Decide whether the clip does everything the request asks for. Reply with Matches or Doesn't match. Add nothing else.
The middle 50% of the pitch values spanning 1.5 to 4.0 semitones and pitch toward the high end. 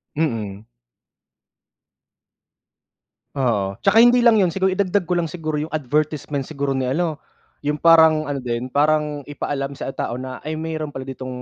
Doesn't match